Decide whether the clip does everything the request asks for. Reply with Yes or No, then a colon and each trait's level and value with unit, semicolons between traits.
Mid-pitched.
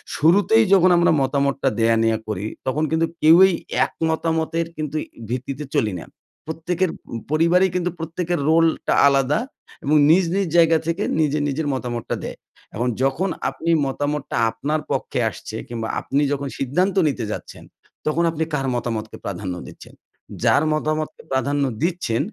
Yes: medium, 155 Hz